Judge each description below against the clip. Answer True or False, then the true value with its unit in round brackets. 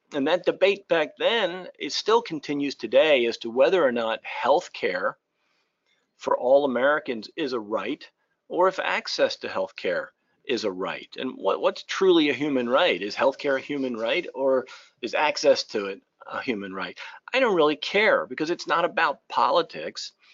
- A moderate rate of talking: True (170 wpm)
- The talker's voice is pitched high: True (200 Hz)